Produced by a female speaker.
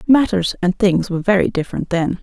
Yes: female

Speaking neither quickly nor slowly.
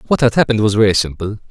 No: fast, 240 wpm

